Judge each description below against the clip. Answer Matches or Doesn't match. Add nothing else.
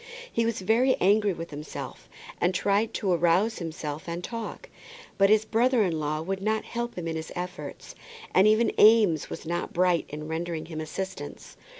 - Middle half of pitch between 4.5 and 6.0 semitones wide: Matches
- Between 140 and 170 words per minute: Doesn't match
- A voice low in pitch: Doesn't match